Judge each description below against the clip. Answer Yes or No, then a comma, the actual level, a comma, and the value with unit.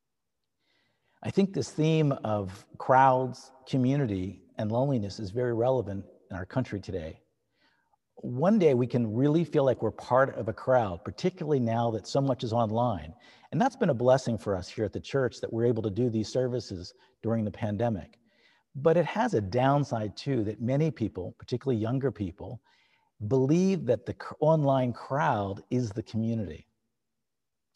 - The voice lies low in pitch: Yes, low, 120 Hz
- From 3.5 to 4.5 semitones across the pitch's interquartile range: Yes, average, 3.8 semitones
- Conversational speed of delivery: Yes, average, 165 wpm